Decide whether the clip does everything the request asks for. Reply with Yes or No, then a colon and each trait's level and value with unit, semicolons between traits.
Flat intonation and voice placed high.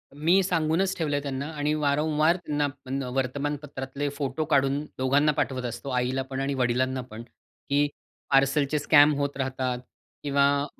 No: narrow, 2.0 semitones; medium, 140 Hz